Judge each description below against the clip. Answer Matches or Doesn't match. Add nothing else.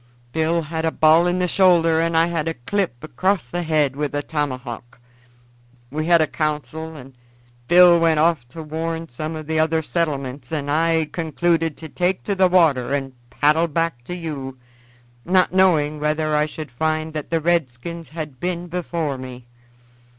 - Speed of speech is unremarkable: Matches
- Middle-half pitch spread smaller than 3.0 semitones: Matches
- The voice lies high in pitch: Doesn't match